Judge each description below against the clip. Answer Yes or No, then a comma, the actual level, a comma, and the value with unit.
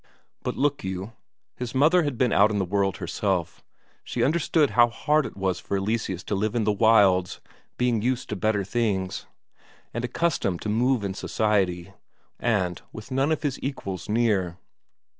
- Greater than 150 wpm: Yes, average, 170 wpm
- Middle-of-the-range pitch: No, low, 110 Hz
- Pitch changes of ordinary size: Yes, average, 4.4 semitones